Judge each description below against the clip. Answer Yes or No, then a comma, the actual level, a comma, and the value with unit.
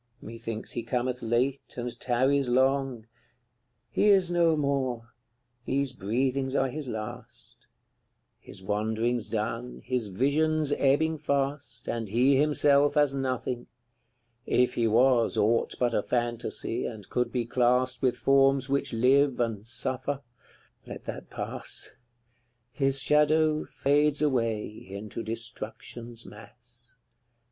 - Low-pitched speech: Yes, low, 125 Hz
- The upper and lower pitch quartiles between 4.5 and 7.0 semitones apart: No, average, 3.2 semitones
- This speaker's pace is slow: Yes, slow, 120 wpm